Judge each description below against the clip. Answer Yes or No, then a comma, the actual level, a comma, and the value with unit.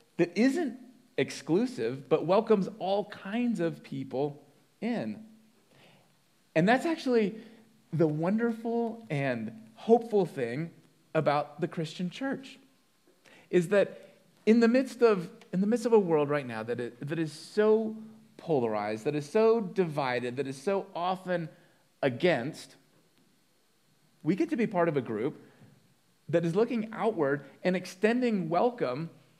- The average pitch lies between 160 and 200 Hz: Yes, medium, 185 Hz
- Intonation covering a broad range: Yes, wide, 6.4 semitones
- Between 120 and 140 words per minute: Yes, slow, 135 wpm